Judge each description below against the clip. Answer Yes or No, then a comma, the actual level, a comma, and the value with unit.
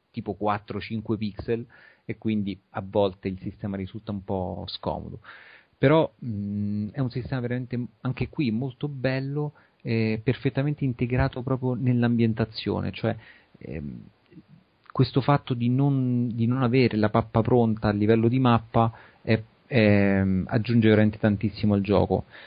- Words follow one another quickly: No, average, 135 wpm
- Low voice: Yes, low, 115 Hz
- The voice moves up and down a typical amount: Yes, average, 3.3 semitones